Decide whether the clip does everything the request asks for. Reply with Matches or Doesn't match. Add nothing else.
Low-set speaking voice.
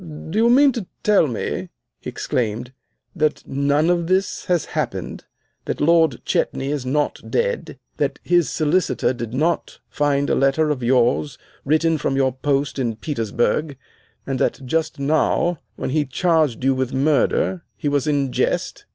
Doesn't match